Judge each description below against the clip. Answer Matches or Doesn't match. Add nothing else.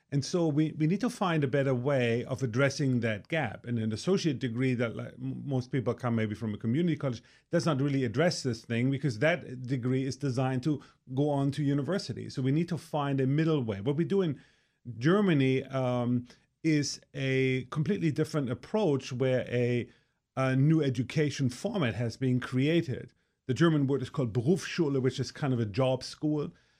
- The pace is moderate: Matches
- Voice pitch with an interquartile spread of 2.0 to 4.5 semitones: Matches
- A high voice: Doesn't match